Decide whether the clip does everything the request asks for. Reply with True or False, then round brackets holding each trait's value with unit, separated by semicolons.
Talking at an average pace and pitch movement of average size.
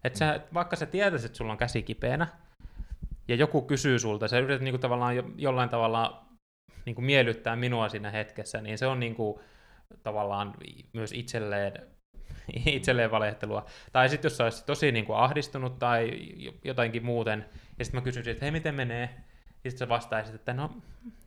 False (165 wpm; 3.2 semitones)